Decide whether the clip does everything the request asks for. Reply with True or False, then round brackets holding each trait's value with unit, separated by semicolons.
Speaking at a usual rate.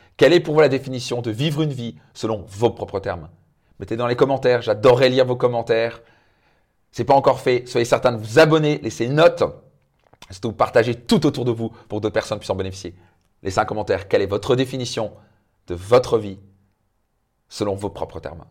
True (200 wpm)